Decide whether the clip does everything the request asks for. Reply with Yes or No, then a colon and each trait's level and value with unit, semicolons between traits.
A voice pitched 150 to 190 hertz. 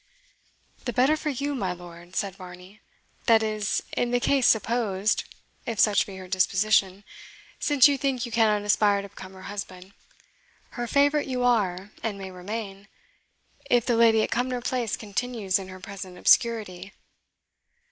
No: high, 210 Hz